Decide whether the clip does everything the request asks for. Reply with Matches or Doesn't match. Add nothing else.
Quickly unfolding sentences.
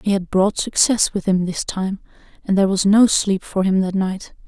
Matches